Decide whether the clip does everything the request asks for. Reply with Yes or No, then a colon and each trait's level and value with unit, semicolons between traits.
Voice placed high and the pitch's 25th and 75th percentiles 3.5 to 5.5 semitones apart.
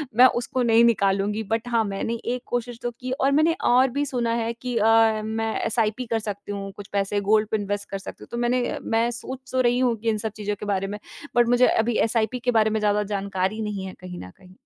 No: high, 225 Hz; average, 2.8 semitones